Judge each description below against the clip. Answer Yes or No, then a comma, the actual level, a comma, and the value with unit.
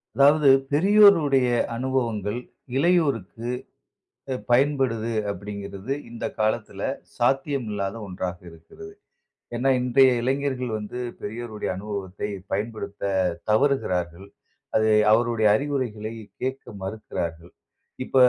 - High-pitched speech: No, low, 115 Hz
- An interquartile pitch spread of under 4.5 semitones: No, average, 5.0 semitones